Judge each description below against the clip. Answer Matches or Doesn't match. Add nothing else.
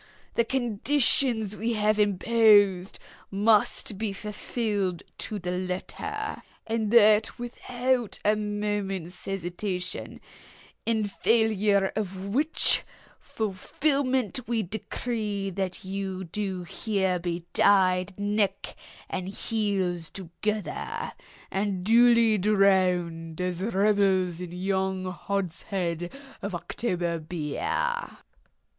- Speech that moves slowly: Matches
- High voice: Matches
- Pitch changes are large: Doesn't match